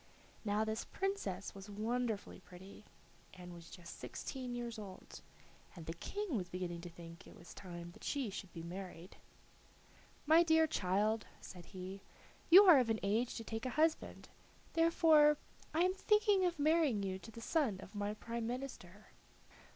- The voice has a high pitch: Yes, high, 220 Hz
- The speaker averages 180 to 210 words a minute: No, average, 165 wpm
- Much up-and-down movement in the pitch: Yes, wide, 8.1 semitones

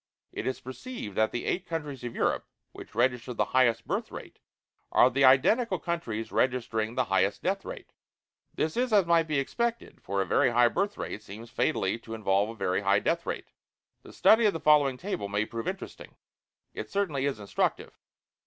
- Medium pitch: No, low, 130 Hz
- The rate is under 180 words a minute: No, average, 190 wpm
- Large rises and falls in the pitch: Yes, wide, 7.1 semitones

